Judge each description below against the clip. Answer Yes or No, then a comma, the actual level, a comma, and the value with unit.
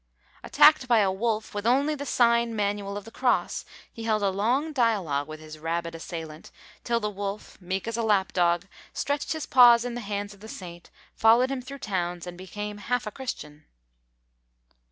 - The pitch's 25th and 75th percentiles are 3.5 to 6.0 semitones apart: Yes, average, 4.6 semitones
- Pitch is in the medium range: No, high, 210 Hz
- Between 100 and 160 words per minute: No, average, 190 wpm